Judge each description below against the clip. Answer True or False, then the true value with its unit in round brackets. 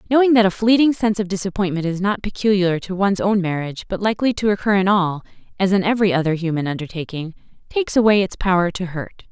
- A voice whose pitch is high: True (195 Hz)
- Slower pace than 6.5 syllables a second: False (6.7 syllables/s)